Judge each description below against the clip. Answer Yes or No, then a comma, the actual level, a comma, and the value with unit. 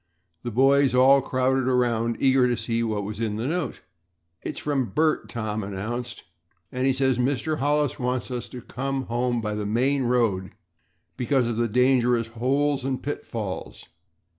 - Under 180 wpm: Yes, average, 165 wpm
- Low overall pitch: Yes, low, 125 Hz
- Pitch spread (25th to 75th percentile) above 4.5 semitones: No, narrow, 2.6 semitones